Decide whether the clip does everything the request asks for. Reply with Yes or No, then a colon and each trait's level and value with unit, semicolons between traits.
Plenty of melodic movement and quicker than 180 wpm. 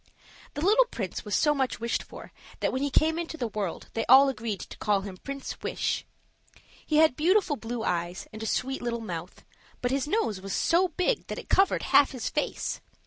Yes: wide, 6.5 semitones; average, 200 wpm